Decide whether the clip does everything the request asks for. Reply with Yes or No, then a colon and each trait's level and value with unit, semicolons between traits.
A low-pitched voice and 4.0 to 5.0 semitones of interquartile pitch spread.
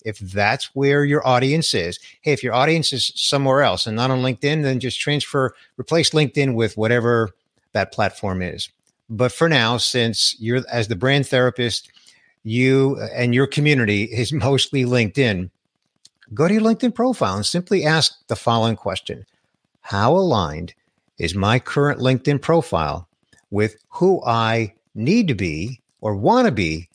Yes: low, 125 Hz; average, 4.6 semitones